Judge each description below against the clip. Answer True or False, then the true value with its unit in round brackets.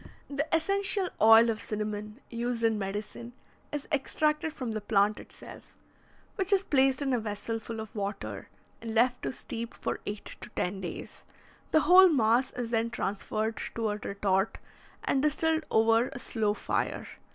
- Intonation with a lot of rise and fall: False (4.6 semitones)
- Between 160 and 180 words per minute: True (165 wpm)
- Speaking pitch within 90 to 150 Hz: False (230 Hz)